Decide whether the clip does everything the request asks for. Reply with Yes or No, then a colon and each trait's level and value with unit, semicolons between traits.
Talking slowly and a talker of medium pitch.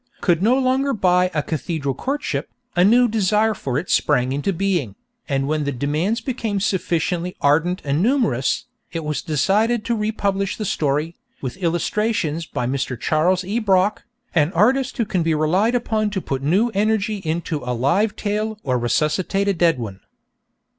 No: average, 165 wpm; medium, 180 Hz